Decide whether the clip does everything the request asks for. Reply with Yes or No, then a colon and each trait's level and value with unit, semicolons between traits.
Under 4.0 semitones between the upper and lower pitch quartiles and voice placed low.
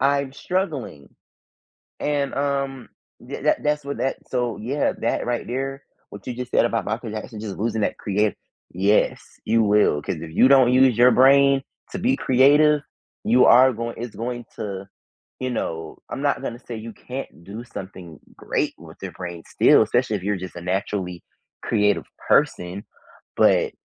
No: average, 4.7 semitones; low, 120 Hz